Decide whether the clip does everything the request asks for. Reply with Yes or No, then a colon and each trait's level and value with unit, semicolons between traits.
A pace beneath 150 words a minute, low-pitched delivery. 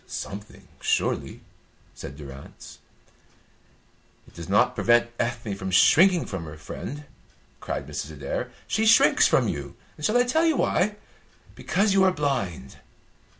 Yes: slow, 135 wpm; low, 120 Hz